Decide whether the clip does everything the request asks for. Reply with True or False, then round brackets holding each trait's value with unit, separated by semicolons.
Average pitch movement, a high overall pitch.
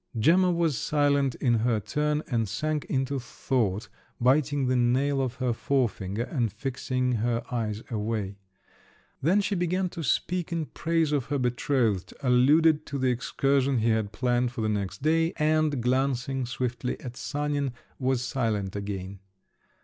False (4.1 semitones; 130 Hz)